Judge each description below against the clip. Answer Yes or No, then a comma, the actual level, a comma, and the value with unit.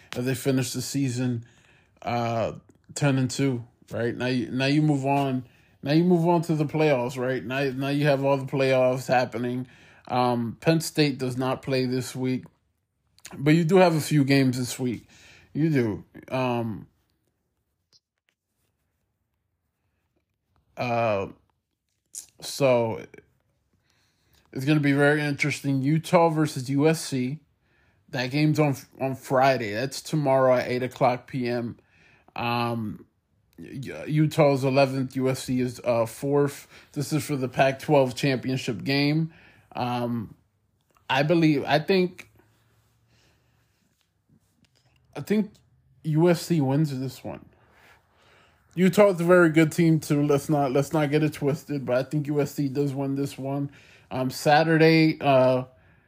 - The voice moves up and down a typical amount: Yes, average, 3.1 semitones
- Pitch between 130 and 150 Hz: Yes, low, 135 Hz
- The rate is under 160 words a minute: Yes, slow, 135 wpm